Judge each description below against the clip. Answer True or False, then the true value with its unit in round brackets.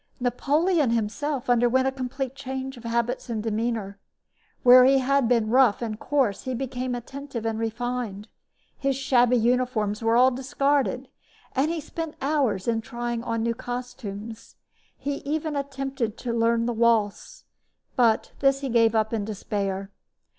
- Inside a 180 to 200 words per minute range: False (150 wpm)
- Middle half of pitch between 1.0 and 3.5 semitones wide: True (2.9 semitones)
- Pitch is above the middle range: True (245 Hz)